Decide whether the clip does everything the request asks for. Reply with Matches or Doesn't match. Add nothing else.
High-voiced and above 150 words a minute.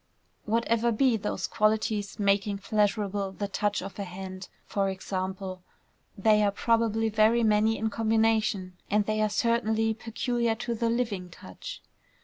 Doesn't match